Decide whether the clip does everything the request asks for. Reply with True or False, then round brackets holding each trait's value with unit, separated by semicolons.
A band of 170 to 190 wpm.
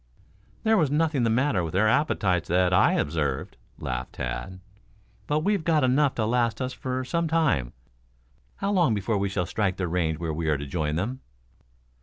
True (185 wpm)